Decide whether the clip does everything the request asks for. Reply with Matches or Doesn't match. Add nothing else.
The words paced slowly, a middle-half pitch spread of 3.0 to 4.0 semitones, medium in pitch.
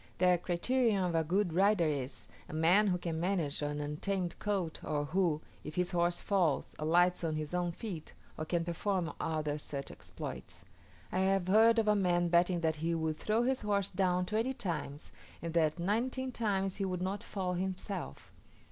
Doesn't match